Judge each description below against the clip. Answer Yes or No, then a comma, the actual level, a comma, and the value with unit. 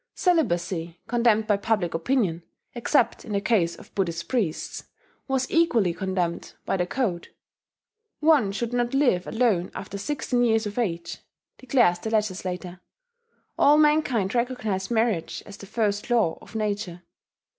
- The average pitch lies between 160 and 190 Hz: No, high, 210 Hz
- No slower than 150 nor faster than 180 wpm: No, average, 140 wpm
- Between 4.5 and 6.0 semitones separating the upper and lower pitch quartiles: Yes, average, 5.1 semitones